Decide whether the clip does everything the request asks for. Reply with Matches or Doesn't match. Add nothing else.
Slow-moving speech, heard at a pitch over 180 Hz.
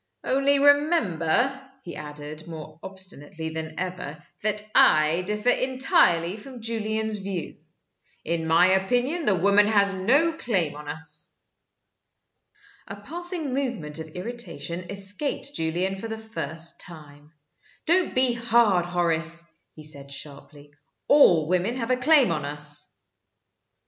Matches